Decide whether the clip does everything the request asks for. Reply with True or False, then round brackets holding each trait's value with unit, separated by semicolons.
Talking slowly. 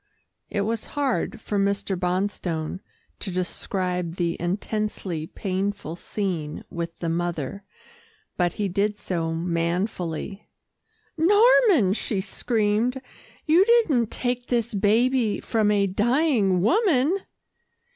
True (105 wpm)